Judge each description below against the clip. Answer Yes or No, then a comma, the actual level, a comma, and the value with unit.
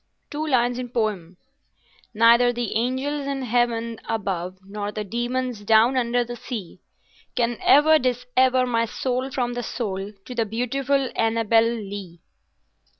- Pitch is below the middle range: No, high, 240 Hz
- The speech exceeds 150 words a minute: No, average, 140 wpm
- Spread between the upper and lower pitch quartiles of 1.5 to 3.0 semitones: Yes, narrow, 2.6 semitones